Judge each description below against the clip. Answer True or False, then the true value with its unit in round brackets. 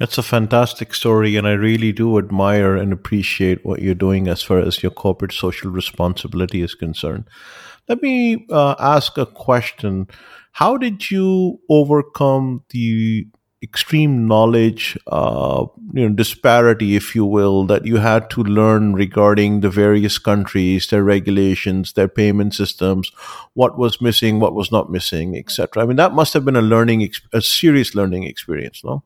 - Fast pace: False (165 wpm)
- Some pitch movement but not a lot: True (3.8 semitones)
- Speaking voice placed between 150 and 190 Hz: False (105 Hz)